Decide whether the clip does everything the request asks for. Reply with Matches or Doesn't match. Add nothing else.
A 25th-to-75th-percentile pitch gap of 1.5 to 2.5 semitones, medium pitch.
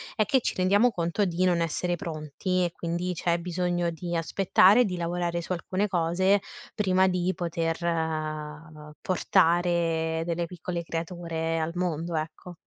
Matches